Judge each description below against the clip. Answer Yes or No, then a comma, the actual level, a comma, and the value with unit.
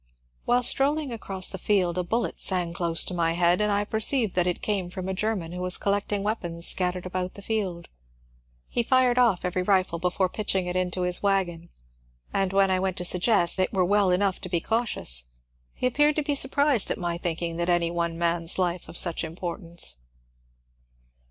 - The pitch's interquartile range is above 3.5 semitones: No, average, 3.1 semitones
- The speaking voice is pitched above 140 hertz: Yes, medium, 185 Hz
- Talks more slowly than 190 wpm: No, average, 195 wpm